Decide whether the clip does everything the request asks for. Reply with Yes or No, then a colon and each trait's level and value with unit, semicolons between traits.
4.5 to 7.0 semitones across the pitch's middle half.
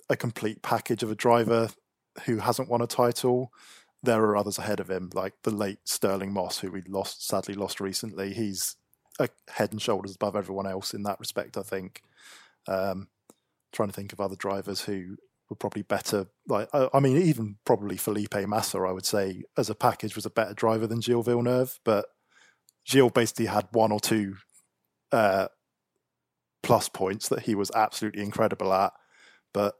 No: average, 2.7 semitones